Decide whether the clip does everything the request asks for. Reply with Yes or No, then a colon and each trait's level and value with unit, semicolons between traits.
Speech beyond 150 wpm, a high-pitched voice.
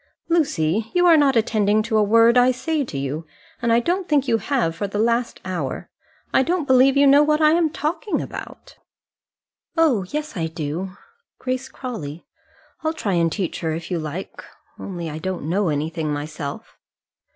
Yes: average, 180 wpm; high, 220 Hz